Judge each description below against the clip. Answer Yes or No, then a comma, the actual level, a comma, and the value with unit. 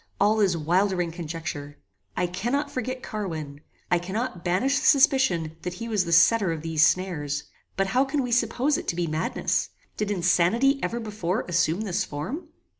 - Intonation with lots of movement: Yes, wide, 5.7 semitones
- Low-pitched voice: No, medium, 185 Hz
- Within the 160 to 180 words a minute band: Yes, average, 175 wpm